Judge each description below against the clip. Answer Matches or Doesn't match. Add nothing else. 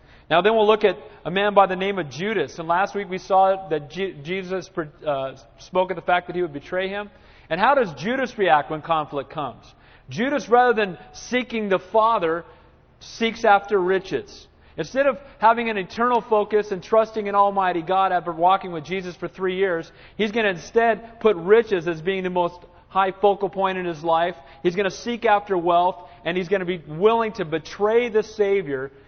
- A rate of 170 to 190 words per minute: Doesn't match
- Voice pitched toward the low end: Doesn't match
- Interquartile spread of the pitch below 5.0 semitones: Matches